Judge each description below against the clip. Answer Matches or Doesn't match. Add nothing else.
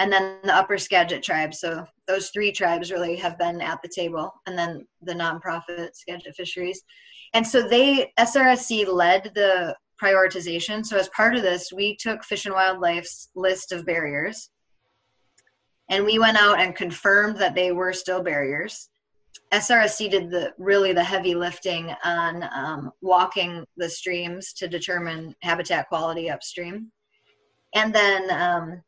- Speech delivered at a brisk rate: Doesn't match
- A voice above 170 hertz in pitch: Matches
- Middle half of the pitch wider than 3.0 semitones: Doesn't match